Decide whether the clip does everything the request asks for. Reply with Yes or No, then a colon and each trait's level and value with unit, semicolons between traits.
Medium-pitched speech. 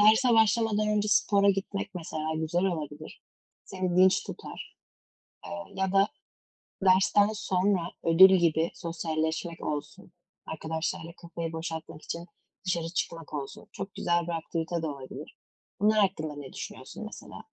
Yes: medium, 175 Hz